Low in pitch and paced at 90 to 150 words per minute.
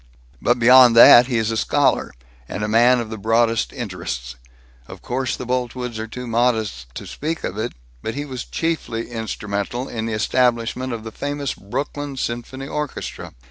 No: low, 120 Hz; average, 175 wpm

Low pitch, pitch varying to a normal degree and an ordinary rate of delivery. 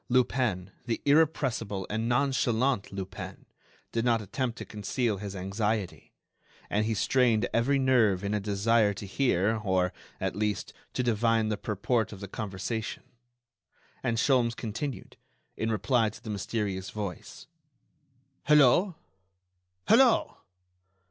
No: low, 110 Hz; average, 3.6 semitones; slow, 125 wpm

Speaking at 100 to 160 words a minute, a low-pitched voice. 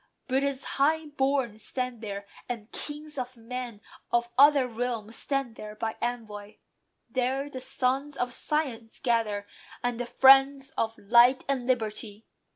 No: average, 140 wpm; very high, 250 Hz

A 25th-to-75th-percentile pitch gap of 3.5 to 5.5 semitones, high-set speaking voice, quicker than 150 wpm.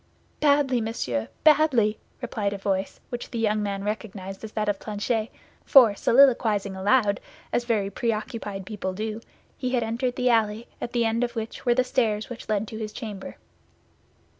No: average, 2.7 semitones; high, 220 Hz; average, 170 wpm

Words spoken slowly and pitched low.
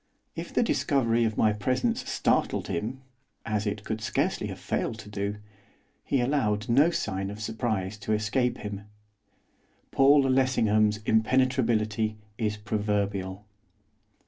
Yes: slow, 125 wpm; low, 110 Hz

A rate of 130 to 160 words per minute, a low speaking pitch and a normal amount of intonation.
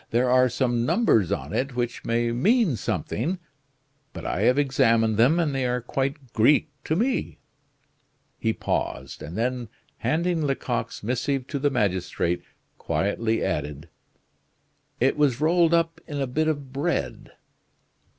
Yes: average, 140 wpm; low, 130 Hz; average, 4.5 semitones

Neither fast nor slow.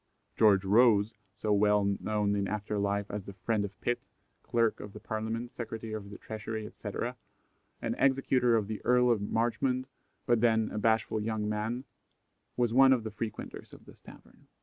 Yes: average, 175 wpm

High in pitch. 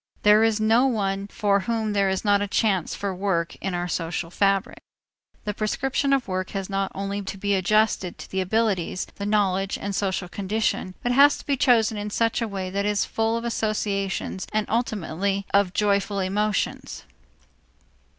Yes: high, 200 Hz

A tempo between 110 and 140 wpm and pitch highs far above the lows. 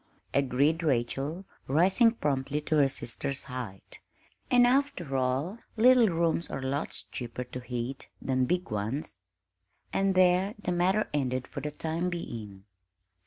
Yes: slow, 135 wpm; wide, 5.8 semitones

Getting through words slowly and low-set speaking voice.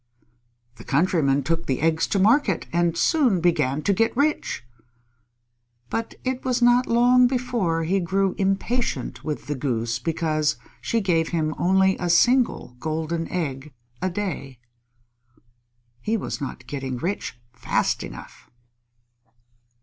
No: slow, 130 wpm; medium, 170 Hz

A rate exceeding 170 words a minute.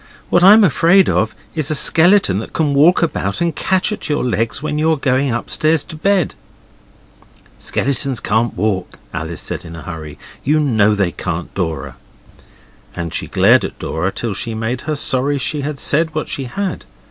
Yes: average, 180 wpm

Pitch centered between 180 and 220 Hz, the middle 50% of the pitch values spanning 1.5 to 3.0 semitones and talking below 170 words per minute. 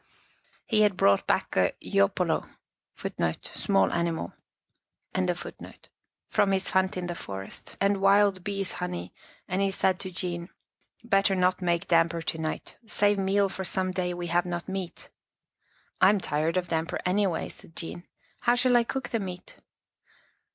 Yes: medium, 185 Hz; narrow, 2.5 semitones; average, 160 wpm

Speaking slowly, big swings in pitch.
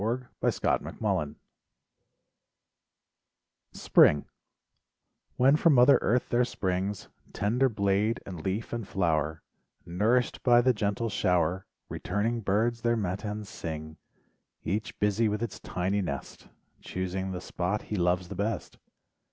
No: slow, 130 wpm; average, 4.2 semitones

